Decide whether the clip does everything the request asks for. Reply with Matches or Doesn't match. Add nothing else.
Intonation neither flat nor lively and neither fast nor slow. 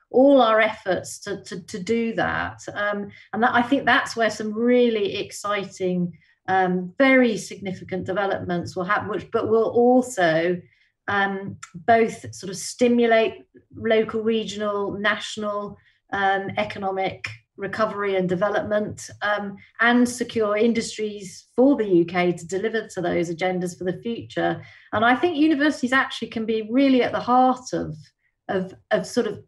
Matches